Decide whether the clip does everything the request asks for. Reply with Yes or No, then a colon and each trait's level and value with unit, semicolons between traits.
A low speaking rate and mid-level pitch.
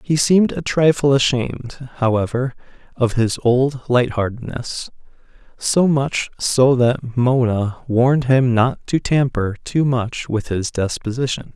No: slow, 130 wpm; low, 125 Hz